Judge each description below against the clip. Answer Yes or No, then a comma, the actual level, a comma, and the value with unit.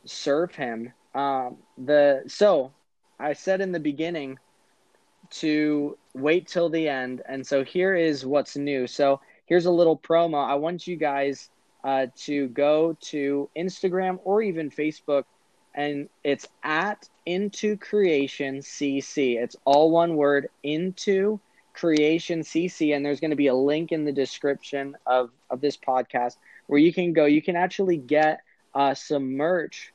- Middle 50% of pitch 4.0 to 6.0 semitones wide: No, average, 3.4 semitones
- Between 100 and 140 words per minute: No, average, 150 wpm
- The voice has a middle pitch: Yes, medium, 150 Hz